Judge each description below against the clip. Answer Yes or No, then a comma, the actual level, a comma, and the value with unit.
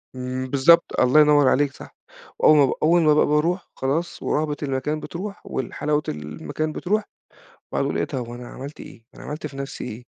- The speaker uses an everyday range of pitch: Yes, average, 3.0 semitones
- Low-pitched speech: No, medium, 145 Hz